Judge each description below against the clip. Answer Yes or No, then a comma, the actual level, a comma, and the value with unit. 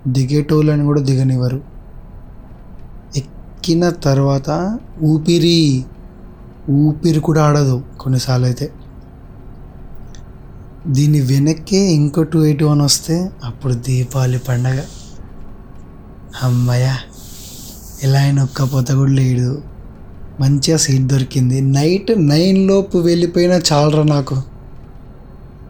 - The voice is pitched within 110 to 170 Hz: Yes, medium, 140 Hz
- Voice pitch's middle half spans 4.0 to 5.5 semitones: No, average, 3.2 semitones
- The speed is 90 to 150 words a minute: No, average, 80 wpm